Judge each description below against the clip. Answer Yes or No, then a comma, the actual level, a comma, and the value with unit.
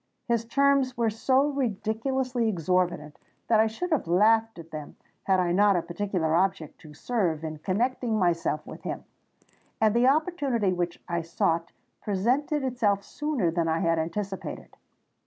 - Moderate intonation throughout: No, wide, 6.3 semitones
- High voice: Yes, high, 205 Hz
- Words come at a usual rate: Yes, average, 155 wpm